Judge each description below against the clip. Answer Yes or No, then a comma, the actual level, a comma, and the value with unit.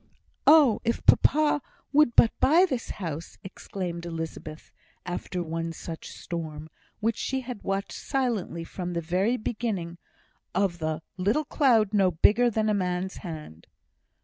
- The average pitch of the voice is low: No, high, 190 Hz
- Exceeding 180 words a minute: No, average, 140 wpm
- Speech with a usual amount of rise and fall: No, wide, 5.7 semitones